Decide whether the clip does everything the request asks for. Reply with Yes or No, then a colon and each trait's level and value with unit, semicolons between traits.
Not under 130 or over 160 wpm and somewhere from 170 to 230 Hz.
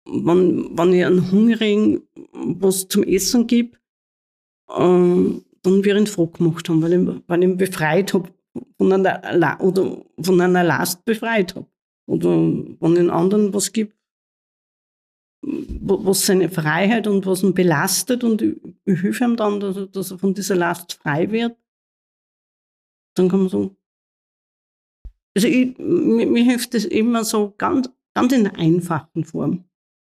Yes: average, 150 wpm; high, 190 Hz